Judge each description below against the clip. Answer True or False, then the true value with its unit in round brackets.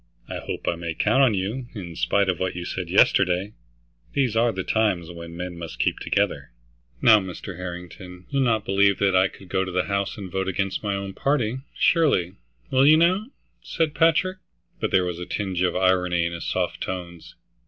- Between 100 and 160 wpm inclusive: False (200 wpm)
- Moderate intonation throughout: True (3.7 semitones)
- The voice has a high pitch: False (95 Hz)